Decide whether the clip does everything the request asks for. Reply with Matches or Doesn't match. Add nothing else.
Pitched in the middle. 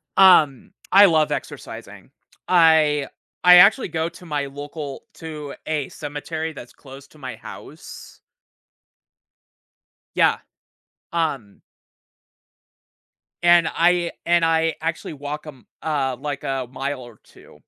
Matches